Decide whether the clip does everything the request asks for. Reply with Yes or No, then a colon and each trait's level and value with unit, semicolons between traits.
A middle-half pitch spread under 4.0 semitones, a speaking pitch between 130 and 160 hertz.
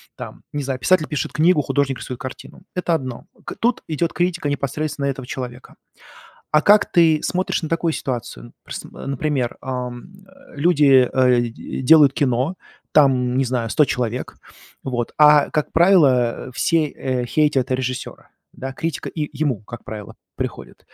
Yes: average, 3.5 semitones; medium, 140 Hz